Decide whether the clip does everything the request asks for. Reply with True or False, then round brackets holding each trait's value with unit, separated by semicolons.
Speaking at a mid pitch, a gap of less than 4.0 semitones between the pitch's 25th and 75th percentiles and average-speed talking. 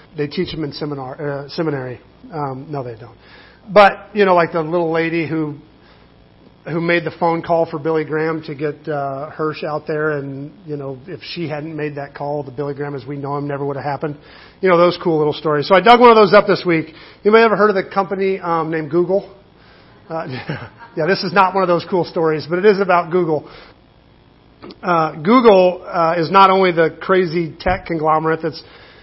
False (160 Hz; 3.4 semitones; 215 wpm)